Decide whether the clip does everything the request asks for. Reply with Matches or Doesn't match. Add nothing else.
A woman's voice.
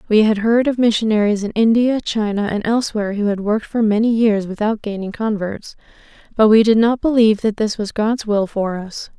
Matches